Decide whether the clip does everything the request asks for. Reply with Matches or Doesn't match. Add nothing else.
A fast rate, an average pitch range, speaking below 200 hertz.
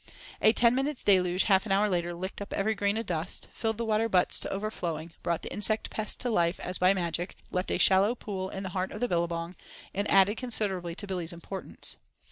Matches